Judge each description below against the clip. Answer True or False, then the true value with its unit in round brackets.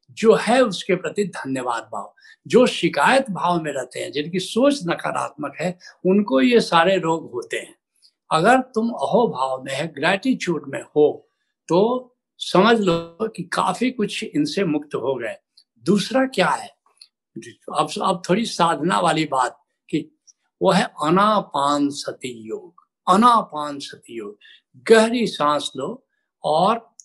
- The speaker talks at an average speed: True (140 wpm)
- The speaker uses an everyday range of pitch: False (7.1 semitones)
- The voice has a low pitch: False (190 Hz)